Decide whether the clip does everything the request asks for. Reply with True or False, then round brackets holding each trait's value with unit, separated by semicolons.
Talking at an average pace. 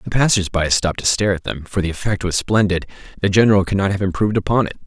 False (245 wpm)